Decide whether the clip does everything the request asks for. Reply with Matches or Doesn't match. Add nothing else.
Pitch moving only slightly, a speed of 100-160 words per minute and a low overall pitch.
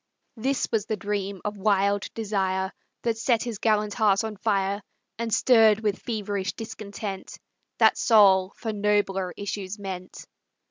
Doesn't match